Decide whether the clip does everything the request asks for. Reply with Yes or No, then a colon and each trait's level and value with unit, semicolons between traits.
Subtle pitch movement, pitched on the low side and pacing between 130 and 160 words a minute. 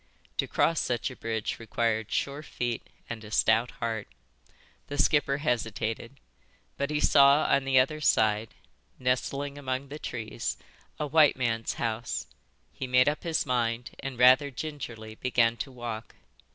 No: average, 3.5 semitones; low, 125 Hz; average, 150 wpm